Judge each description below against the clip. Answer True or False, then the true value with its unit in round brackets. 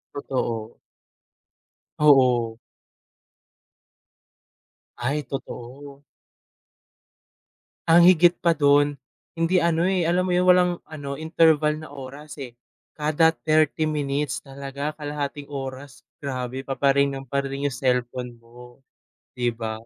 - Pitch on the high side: False (140 Hz)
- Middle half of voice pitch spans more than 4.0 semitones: False (3.2 semitones)